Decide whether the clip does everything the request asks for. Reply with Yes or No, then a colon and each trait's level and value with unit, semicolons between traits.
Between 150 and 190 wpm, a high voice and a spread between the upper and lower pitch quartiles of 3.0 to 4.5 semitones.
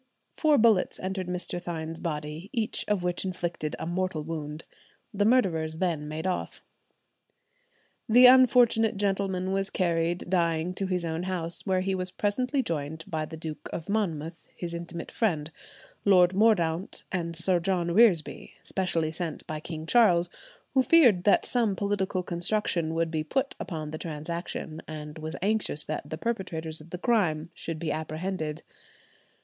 No: average, 155 wpm; medium, 175 Hz; average, 3.4 semitones